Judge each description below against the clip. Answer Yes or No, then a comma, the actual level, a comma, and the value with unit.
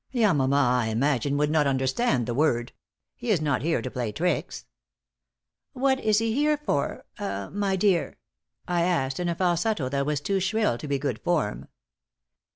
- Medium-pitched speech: Yes, medium, 150 Hz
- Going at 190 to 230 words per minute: No, average, 170 wpm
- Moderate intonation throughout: No, wide, 6.9 semitones